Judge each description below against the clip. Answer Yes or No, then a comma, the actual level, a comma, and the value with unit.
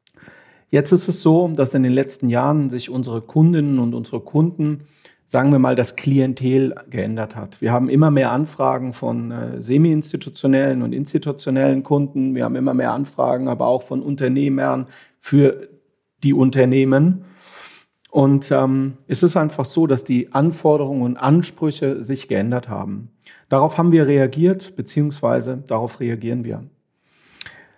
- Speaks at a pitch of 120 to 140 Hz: Yes, low, 135 Hz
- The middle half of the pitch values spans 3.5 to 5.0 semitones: No, average, 2.9 semitones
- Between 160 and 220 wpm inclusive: No, average, 145 wpm